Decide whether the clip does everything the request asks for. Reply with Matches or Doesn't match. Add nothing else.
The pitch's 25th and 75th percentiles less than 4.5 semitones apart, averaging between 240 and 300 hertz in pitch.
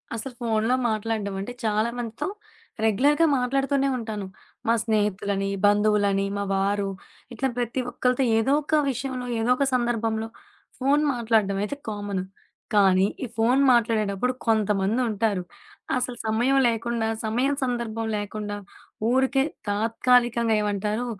Doesn't match